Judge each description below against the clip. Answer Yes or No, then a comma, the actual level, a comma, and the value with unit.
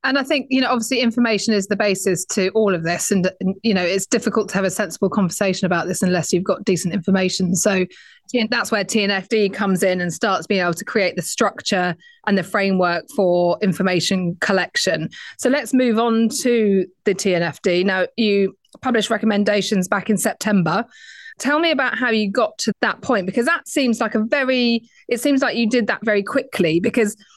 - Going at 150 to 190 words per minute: No, average, 200 wpm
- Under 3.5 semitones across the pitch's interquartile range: No, average, 4.1 semitones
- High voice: Yes, high, 205 Hz